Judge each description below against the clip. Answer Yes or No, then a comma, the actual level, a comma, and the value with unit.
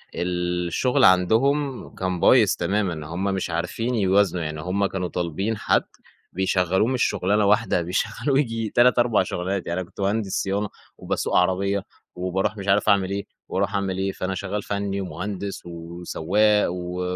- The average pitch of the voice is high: No, very low, 95 Hz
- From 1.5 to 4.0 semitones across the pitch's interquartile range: Yes, narrow, 2.6 semitones